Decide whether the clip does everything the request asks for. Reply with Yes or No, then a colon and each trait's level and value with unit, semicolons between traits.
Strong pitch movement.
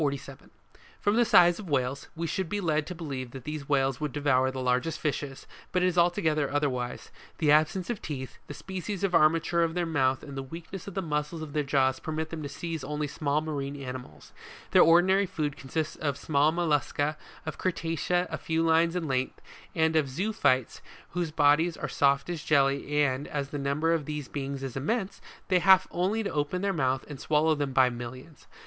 No: average, 3.4 semitones